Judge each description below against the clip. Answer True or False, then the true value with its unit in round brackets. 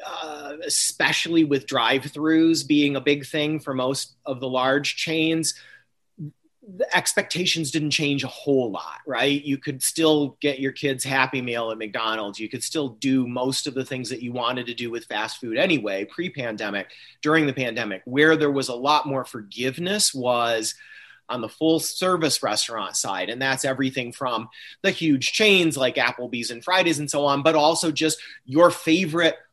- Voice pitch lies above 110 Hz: True (140 Hz)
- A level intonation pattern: False (3.8 semitones)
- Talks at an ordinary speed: True (180 wpm)